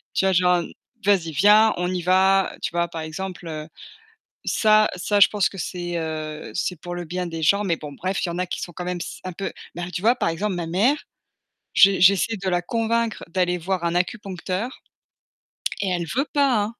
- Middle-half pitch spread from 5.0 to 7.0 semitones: No, average, 2.7 semitones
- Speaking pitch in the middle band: Yes, medium, 180 Hz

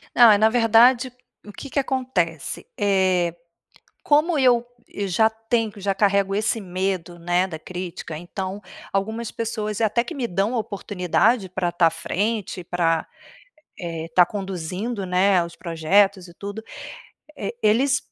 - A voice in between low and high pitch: No, high, 200 Hz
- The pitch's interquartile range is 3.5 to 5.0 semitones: Yes, average, 4.0 semitones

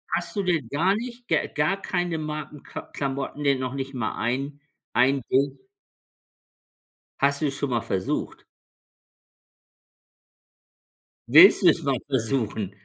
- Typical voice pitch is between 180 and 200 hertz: No, medium, 140 Hz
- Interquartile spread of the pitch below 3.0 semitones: No, average, 3.7 semitones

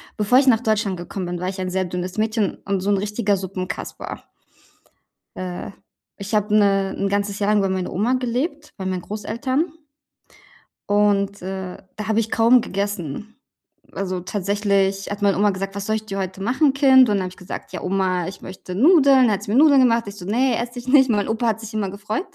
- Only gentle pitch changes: No, average, 3.1 semitones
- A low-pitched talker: No, high, 205 Hz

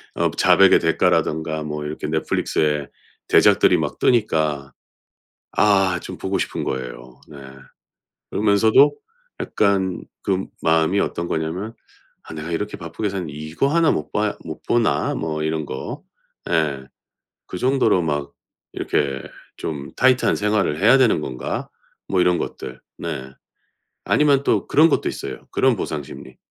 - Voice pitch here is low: Yes, very low, 80 Hz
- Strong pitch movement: Yes, wide, 5.8 semitones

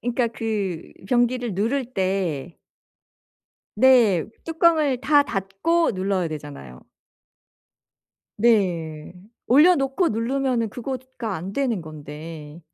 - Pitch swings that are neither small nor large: No, wide, 7.0 semitones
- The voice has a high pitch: Yes, high, 225 Hz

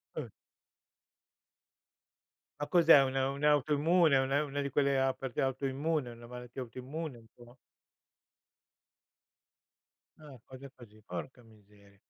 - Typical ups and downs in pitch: Yes, average, 3.0 semitones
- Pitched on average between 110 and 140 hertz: Yes, low, 135 Hz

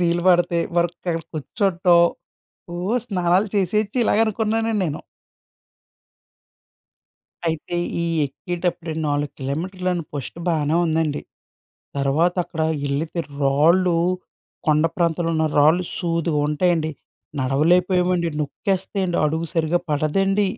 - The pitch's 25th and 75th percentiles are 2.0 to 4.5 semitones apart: Yes, average, 2.8 semitones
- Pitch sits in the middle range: Yes, medium, 170 Hz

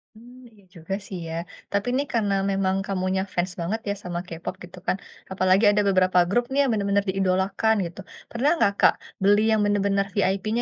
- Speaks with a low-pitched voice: No, high, 195 Hz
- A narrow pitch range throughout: Yes, narrow, 2.3 semitones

